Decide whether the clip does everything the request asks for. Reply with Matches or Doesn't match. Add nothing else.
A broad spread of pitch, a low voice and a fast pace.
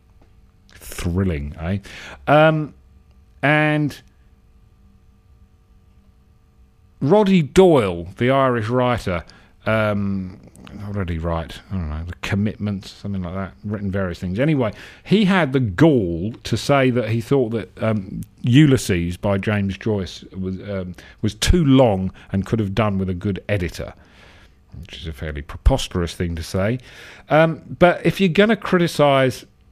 Doesn't match